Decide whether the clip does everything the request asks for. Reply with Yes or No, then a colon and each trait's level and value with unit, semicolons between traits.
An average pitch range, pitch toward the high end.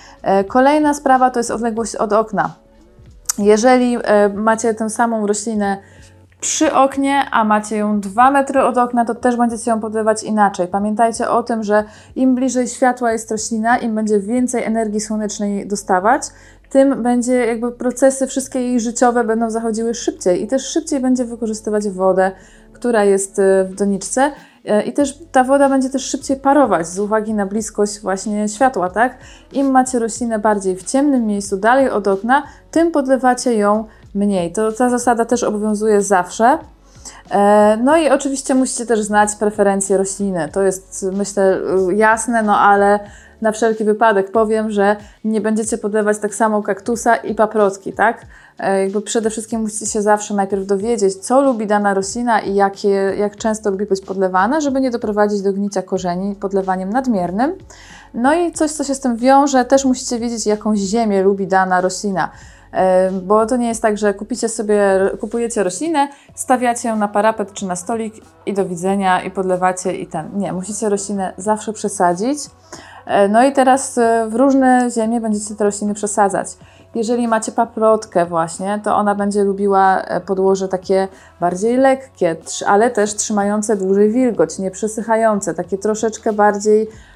Yes: average, 3.3 semitones; high, 220 Hz